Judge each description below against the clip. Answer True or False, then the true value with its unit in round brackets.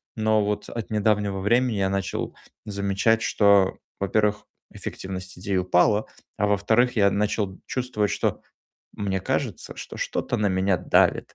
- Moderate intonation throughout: False (1.8 semitones)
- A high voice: False (100 Hz)